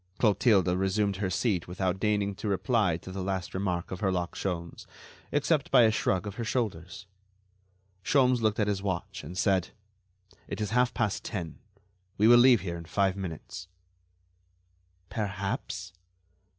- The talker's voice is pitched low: Yes, very low, 95 Hz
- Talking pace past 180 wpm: No, average, 150 wpm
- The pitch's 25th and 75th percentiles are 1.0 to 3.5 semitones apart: Yes, average, 2.8 semitones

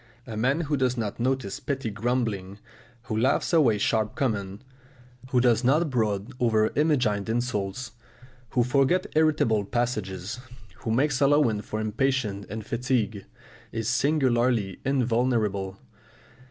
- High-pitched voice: No, low, 120 Hz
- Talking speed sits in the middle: No, slow, 125 wpm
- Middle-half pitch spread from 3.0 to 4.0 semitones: Yes, average, 3.7 semitones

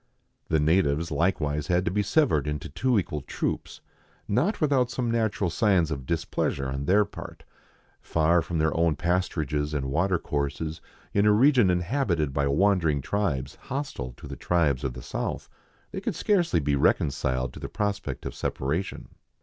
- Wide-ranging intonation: Yes, wide, 5.8 semitones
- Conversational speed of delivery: Yes, average, 165 wpm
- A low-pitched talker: Yes, very low, 85 Hz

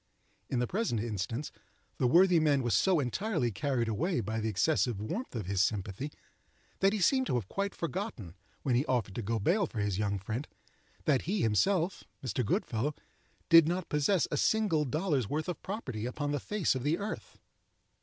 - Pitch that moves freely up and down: Yes, wide, 7.9 semitones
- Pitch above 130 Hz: Yes, medium, 140 Hz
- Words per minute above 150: Yes, average, 185 wpm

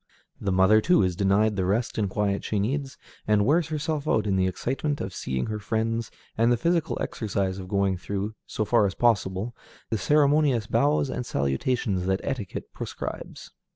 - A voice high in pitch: No, low, 110 Hz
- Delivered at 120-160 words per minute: No, average, 180 wpm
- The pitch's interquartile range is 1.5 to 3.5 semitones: No, average, 4.8 semitones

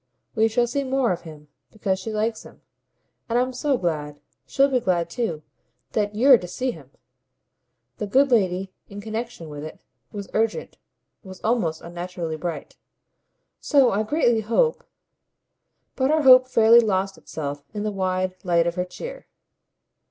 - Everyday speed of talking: Yes, average, 160 wpm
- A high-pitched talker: Yes, high, 210 Hz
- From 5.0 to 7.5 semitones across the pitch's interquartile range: Yes, wide, 5.6 semitones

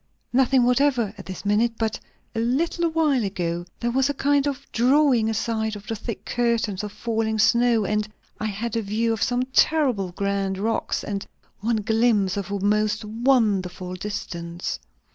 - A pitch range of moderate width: Yes, average, 3.3 semitones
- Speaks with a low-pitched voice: No, high, 220 Hz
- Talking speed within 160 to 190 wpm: Yes, average, 165 wpm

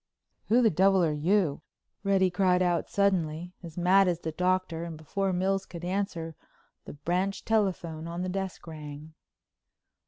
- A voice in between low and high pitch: Yes, medium, 180 Hz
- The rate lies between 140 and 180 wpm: Yes, average, 155 wpm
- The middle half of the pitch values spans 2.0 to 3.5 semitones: Yes, average, 2.9 semitones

